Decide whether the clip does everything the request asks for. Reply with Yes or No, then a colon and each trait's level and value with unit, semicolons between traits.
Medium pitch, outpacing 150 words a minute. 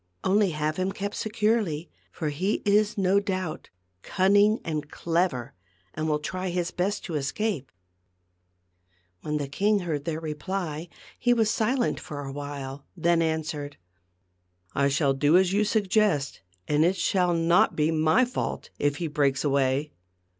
Yes: medium, 165 Hz; average, 160 wpm